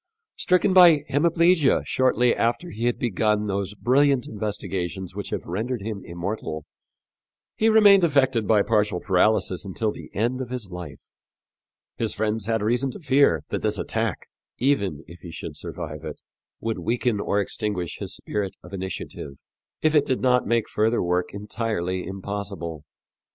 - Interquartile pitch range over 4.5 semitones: Yes, average, 5.1 semitones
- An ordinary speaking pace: Yes, average, 155 wpm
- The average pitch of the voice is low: Yes, low, 110 Hz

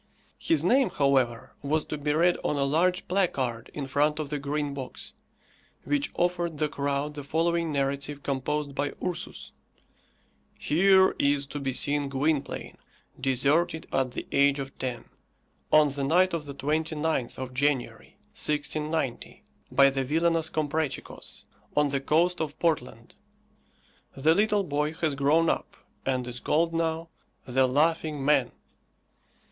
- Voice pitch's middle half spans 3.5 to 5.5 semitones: No, average, 2.8 semitones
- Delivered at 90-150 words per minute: Yes, average, 140 wpm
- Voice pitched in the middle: Yes, medium, 150 Hz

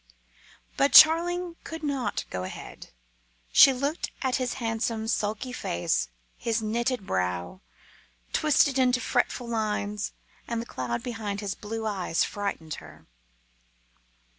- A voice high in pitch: Yes, high, 225 Hz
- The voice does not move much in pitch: No, average, 4.3 semitones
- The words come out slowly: Yes, slow, 120 wpm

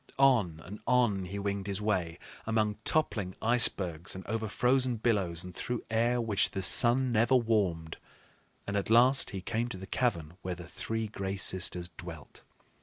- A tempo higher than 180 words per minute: No, average, 170 wpm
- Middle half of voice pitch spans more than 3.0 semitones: Yes, average, 4.4 semitones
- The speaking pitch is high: No, low, 105 Hz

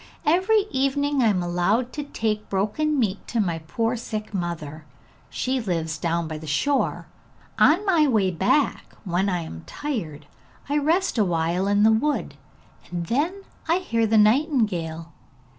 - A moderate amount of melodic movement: No, wide, 8.6 semitones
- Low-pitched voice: No, high, 215 Hz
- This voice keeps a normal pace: Yes, average, 155 wpm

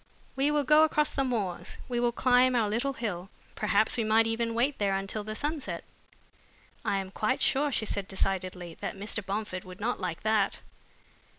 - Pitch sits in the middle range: No, high, 220 Hz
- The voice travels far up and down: No, average, 4.6 semitones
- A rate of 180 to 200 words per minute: Yes, average, 185 wpm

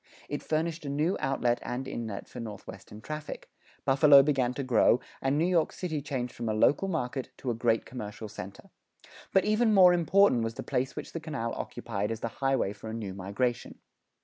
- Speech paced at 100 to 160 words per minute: No, average, 195 wpm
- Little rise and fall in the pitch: No, average, 5.2 semitones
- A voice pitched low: Yes, low, 130 Hz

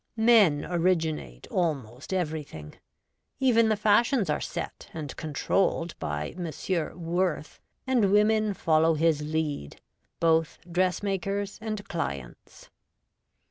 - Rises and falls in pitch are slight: No, average, 4.9 semitones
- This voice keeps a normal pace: No, slow, 100 wpm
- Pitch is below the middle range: No, medium, 170 Hz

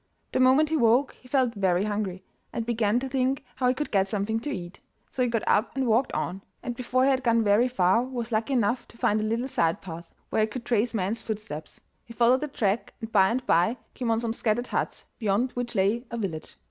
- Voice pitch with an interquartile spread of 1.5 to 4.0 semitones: Yes, average, 3.5 semitones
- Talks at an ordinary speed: No, fast, 235 wpm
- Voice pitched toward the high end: Yes, high, 230 Hz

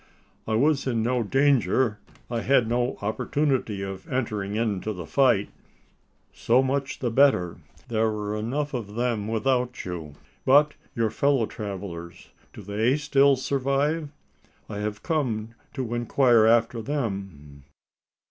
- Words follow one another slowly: Yes, slow, 130 wpm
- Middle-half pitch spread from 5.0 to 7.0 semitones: No, average, 4.4 semitones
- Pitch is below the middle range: Yes, low, 115 Hz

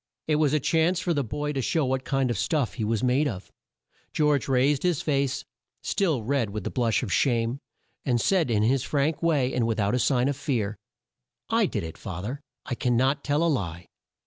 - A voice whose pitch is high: No, low, 130 Hz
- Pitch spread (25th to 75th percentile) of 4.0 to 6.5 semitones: Yes, average, 4.3 semitones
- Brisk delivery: Yes, fast, 220 wpm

